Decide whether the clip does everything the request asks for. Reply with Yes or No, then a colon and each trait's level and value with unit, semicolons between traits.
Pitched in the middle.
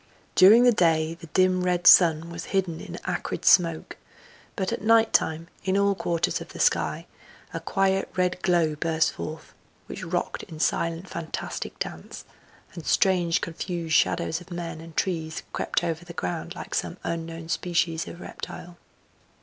Yes: medium, 170 Hz